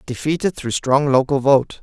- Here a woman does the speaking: No, male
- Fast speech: No, average, 165 wpm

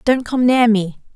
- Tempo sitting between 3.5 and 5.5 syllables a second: Yes, 4.3 syllables/s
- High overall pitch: Yes, high, 230 Hz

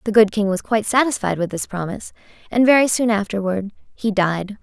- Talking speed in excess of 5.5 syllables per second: Yes, 5.7 syllables/s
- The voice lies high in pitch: Yes, high, 210 Hz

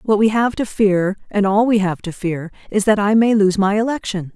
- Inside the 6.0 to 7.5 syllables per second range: No, 5.0 syllables/s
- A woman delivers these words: Yes, female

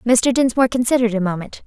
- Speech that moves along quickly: No, average, 180 wpm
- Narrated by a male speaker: No, female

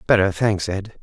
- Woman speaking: No, male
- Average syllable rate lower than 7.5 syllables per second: Yes, 4.6 syllables/s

